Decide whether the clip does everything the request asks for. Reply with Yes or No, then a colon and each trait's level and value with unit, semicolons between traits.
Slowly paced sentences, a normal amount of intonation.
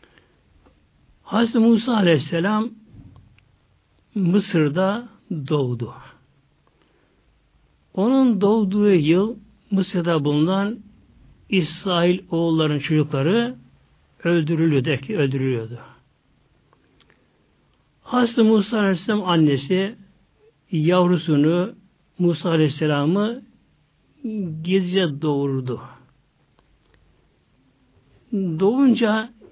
No: slow, 50 wpm; wide, 6.1 semitones